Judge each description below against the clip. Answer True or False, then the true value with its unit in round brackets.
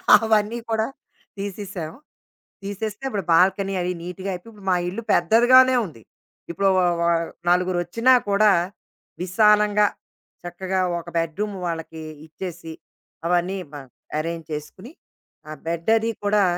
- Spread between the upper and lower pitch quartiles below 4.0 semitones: True (3.3 semitones)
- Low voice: False (195 Hz)